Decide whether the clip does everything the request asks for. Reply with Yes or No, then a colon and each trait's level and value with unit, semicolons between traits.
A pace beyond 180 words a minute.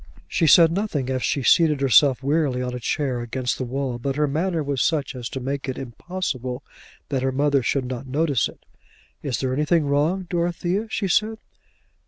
Yes: average, 190 wpm